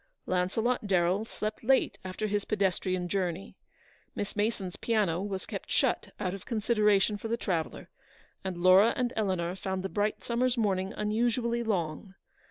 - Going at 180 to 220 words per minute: No, average, 150 wpm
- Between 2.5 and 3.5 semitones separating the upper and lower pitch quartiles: Yes, average, 3.1 semitones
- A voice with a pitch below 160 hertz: No, high, 200 Hz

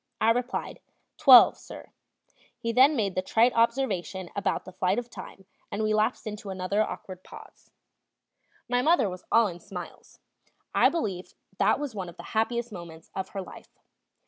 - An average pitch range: Yes, average, 4.3 semitones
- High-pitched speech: Yes, high, 215 Hz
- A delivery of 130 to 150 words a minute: No, average, 170 wpm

